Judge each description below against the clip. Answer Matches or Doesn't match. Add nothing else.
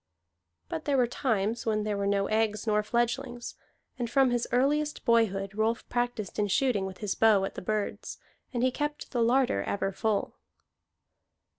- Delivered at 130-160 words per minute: Doesn't match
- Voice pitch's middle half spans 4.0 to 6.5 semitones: Doesn't match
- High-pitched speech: Matches